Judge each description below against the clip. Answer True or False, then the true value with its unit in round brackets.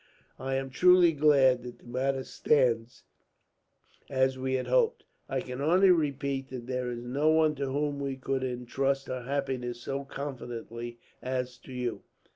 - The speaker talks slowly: False (160 wpm)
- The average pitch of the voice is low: True (130 Hz)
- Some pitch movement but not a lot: False (2.0 semitones)